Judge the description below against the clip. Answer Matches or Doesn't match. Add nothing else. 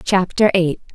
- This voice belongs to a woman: Matches